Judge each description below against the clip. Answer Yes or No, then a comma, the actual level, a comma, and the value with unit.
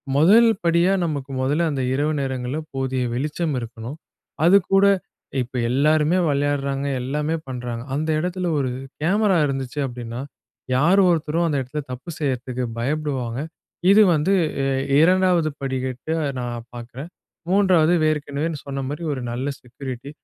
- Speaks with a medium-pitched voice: Yes, medium, 145 Hz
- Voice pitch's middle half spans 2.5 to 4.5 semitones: Yes, average, 4.2 semitones